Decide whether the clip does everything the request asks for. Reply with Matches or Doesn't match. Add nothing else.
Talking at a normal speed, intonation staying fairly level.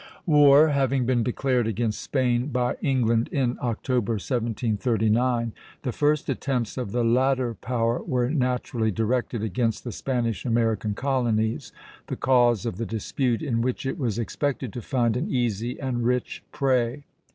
Matches